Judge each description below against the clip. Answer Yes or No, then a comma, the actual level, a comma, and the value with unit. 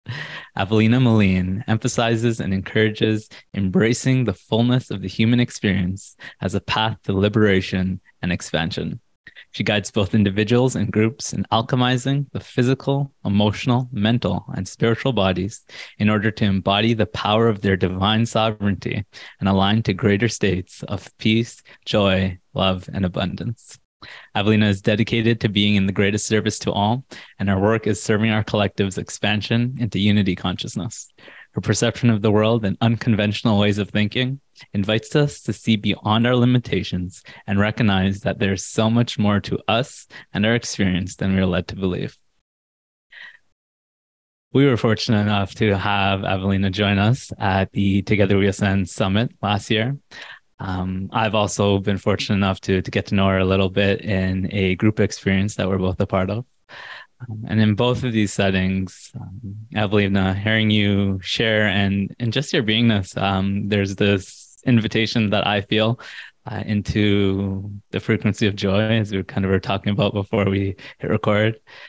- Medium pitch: No, low, 105 Hz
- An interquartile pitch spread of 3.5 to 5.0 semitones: No, narrow, 2.4 semitones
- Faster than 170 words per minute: No, average, 165 wpm